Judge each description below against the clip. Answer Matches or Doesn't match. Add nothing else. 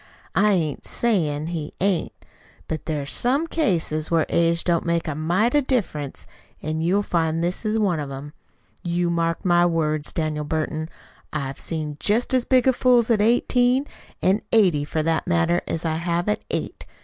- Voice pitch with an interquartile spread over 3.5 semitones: Matches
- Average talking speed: Matches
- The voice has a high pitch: Doesn't match